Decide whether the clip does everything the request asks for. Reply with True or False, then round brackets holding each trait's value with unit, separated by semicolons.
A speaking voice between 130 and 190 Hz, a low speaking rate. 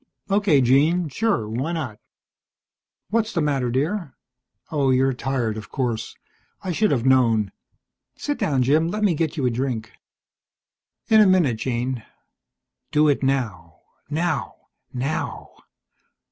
True (135 Hz; 130 wpm)